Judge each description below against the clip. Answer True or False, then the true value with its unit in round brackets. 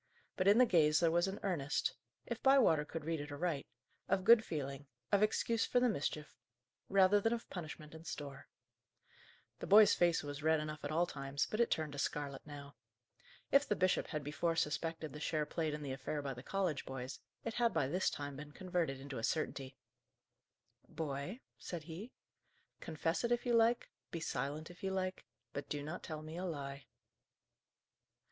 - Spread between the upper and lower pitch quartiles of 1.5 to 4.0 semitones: False (4.6 semitones)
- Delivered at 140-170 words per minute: False (190 wpm)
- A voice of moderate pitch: True (160 Hz)